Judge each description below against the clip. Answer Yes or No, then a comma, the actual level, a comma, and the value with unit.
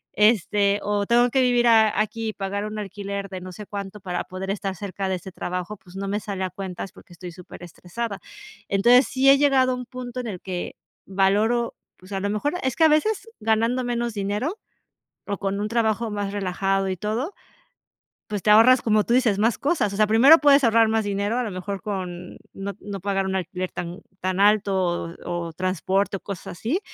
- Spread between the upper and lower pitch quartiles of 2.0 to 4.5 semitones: Yes, average, 3.3 semitones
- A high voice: Yes, high, 205 Hz